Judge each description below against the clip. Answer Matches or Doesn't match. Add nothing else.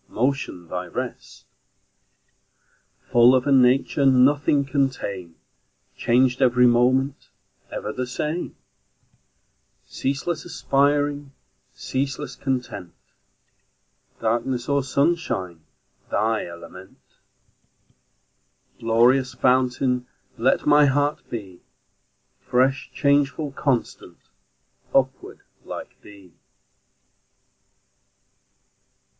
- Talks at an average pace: Doesn't match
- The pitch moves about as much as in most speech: Matches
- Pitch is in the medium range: Doesn't match